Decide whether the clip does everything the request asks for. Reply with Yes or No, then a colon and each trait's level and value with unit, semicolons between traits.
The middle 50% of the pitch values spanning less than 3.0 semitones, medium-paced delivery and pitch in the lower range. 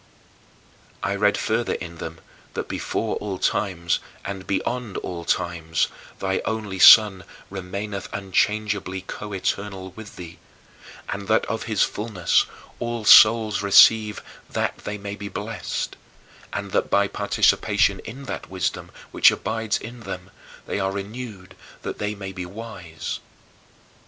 No: narrow, 2.5 semitones; slow, 130 wpm; low, 100 Hz